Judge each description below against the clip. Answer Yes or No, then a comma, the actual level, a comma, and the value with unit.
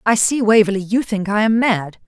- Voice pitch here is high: Yes, high, 210 Hz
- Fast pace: Yes, fast, 230 wpm